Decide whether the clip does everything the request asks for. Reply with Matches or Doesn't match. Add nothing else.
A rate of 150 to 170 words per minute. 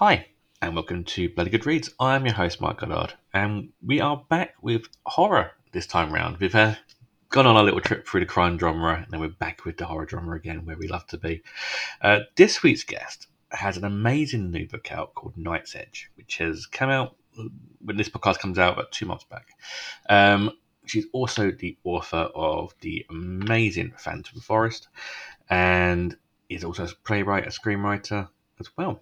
Doesn't match